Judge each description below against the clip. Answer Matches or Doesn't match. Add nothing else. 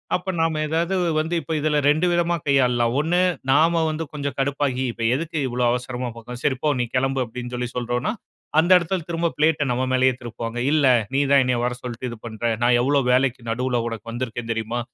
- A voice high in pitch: Doesn't match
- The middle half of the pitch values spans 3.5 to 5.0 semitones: Matches